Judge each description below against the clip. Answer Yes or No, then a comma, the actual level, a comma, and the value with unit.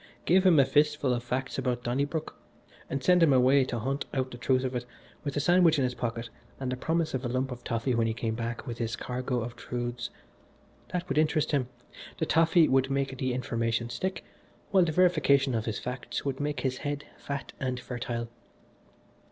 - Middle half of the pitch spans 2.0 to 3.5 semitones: Yes, average, 3.1 semitones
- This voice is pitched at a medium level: No, low, 130 Hz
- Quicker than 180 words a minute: Yes, fast, 205 wpm